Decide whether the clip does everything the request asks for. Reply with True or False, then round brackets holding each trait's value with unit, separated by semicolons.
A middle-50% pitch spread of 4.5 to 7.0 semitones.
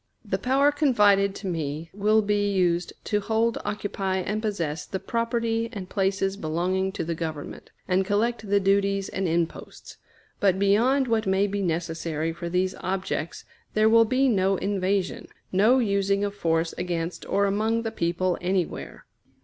False (3.0 semitones)